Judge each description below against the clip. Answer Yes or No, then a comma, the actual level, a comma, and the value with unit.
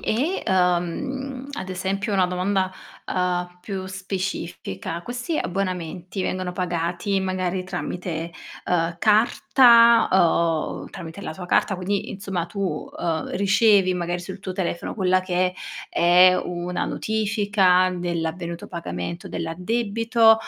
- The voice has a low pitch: No, medium, 185 Hz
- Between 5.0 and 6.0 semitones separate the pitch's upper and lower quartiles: No, narrow, 2.5 semitones